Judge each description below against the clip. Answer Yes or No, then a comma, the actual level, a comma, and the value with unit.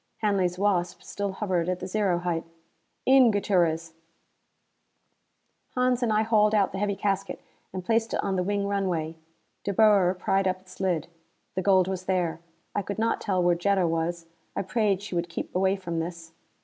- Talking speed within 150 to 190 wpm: Yes, average, 180 wpm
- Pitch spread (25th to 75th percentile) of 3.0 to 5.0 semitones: No, narrow, 2.6 semitones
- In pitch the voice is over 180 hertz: Yes, high, 190 Hz